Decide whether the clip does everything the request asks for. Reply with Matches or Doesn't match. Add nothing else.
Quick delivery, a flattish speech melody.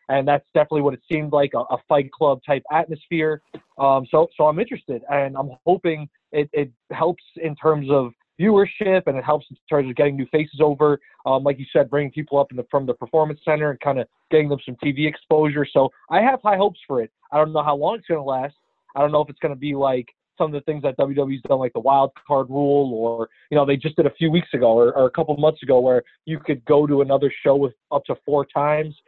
Matches